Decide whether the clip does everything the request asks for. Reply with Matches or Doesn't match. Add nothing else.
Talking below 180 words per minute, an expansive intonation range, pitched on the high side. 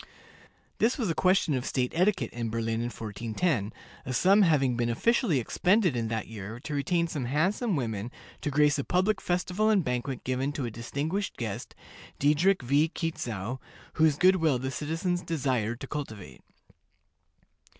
Doesn't match